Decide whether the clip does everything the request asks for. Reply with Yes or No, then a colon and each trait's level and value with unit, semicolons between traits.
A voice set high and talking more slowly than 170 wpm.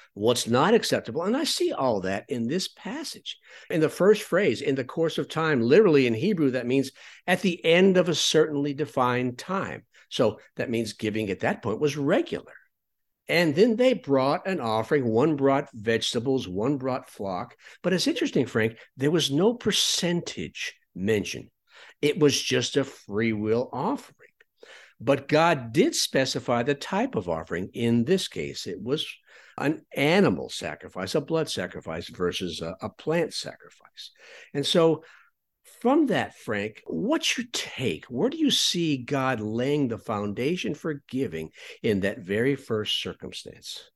No: medium, 140 Hz; average, 160 wpm